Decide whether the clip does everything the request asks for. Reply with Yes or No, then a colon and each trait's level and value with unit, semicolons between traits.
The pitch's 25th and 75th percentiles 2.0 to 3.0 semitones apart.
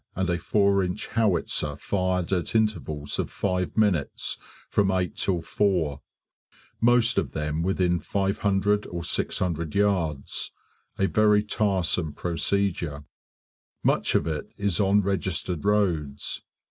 No: average, 3.5 semitones